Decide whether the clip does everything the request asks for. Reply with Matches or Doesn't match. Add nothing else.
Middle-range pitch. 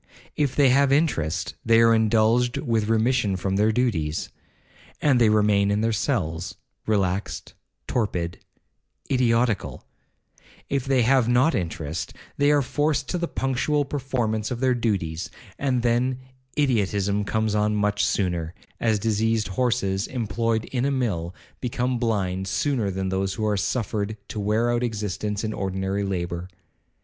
Doesn't match